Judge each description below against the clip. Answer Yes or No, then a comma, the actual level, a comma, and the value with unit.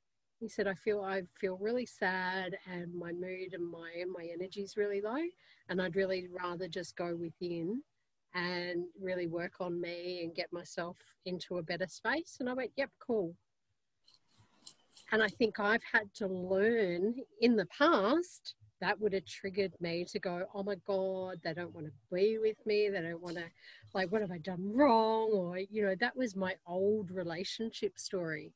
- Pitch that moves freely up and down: No, average, 3.2 semitones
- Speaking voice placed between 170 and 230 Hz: Yes, high, 190 Hz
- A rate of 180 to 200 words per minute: Yes, average, 185 wpm